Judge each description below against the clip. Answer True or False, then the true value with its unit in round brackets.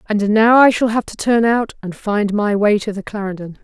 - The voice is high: True (210 Hz)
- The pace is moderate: False (250 wpm)